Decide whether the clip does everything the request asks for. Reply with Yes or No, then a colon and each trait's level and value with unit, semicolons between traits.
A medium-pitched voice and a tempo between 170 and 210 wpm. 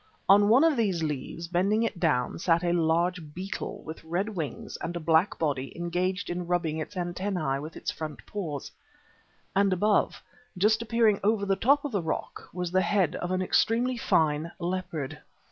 Yes: medium, 180 Hz; average, 180 wpm